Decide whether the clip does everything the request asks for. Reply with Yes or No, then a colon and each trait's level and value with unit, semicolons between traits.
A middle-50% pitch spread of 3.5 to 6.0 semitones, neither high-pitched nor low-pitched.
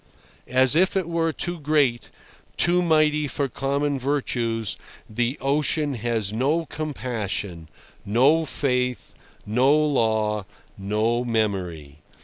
No: average, 5.3 semitones; low, 130 Hz